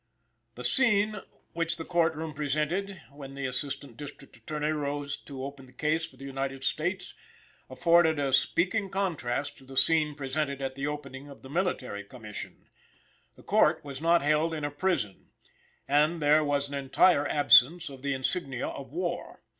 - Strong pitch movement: No, average, 3.3 semitones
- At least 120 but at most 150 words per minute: No, average, 170 wpm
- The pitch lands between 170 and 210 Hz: No, medium, 145 Hz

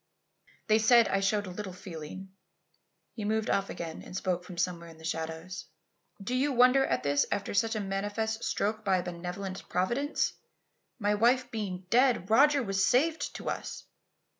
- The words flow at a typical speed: Yes, average, 170 wpm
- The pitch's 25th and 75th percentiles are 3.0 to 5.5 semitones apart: Yes, average, 3.9 semitones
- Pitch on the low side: No, high, 200 Hz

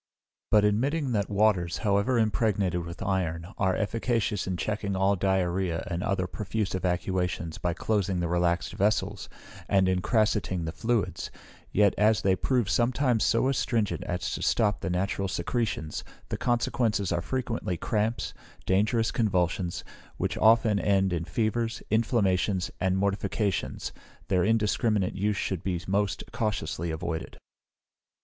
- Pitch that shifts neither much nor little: Yes, average, 3.3 semitones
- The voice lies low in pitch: Yes, low, 100 Hz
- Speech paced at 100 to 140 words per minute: Yes, slow, 135 wpm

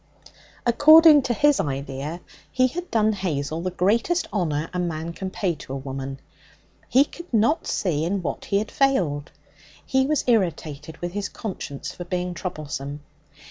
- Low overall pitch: No, medium, 180 Hz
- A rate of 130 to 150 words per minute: No, average, 160 wpm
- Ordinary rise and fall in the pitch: No, wide, 7.7 semitones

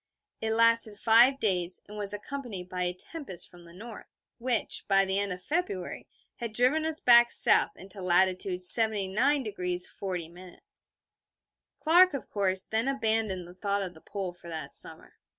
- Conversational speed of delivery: Yes, average, 160 wpm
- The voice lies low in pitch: No, high, 200 Hz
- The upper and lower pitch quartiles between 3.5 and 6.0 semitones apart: Yes, average, 4.1 semitones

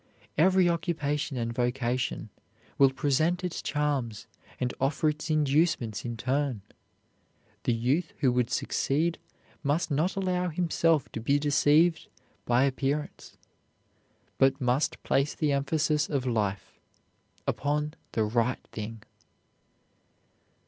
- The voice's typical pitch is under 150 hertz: Yes, medium, 140 Hz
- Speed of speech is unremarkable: No, slow, 115 wpm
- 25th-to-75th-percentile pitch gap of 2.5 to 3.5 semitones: No, average, 4.0 semitones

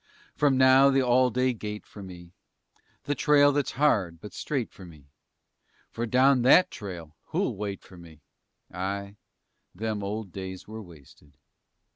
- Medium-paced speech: Yes, average, 150 wpm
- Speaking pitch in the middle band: No, low, 105 Hz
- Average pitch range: No, wide, 5.9 semitones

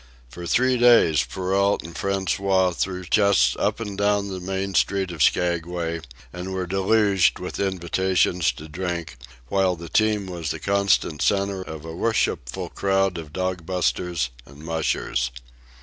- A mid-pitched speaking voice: No, very low, 95 Hz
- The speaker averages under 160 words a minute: Yes, average, 150 wpm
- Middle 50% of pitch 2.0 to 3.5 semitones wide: Yes, narrow, 2.6 semitones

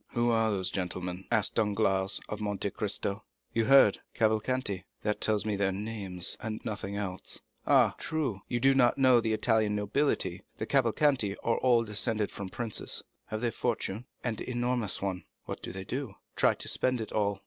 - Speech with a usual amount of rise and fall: Yes, average, 3.3 semitones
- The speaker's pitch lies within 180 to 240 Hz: No, low, 110 Hz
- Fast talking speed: No, average, 175 wpm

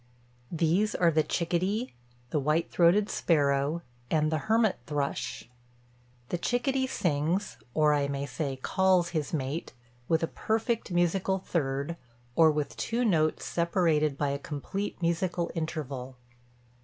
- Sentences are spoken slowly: Yes, slow, 130 wpm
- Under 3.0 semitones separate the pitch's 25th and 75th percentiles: No, average, 4.1 semitones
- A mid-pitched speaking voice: Yes, medium, 165 Hz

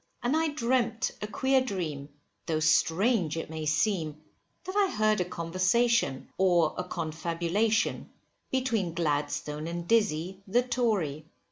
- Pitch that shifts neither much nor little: No, wide, 6.5 semitones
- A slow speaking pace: Yes, slow, 130 wpm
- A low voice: No, medium, 185 Hz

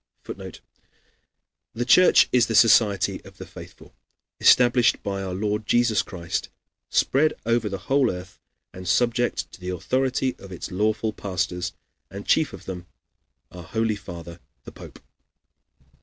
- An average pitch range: Yes, average, 4.8 semitones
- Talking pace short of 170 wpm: Yes, average, 140 wpm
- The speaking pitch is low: Yes, low, 105 Hz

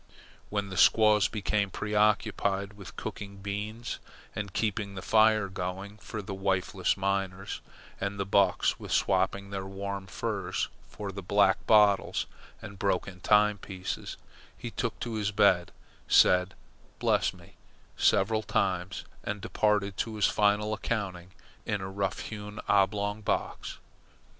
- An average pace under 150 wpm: Yes, slow, 135 wpm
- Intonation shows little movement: Yes, narrow, 1.5 semitones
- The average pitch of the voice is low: Yes, low, 100 Hz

